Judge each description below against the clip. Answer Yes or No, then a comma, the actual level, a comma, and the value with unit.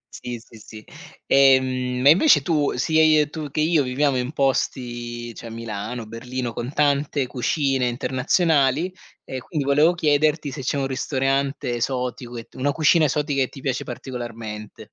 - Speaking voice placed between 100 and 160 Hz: Yes, low, 135 Hz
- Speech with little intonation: No, average, 3.2 semitones